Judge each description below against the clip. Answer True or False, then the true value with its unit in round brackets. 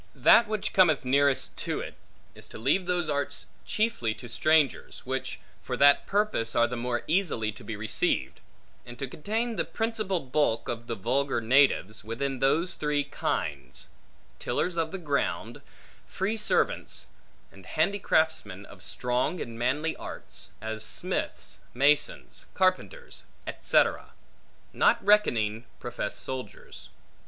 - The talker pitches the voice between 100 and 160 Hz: True (140 Hz)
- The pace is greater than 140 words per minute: False (135 wpm)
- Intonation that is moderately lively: False (7.3 semitones)